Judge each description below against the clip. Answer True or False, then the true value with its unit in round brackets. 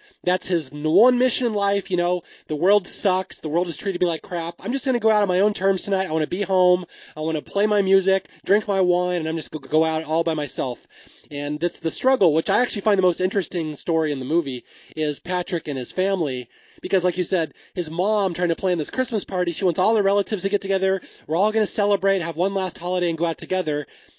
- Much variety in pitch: False (3.4 semitones)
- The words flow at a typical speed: False (255 wpm)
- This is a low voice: False (180 Hz)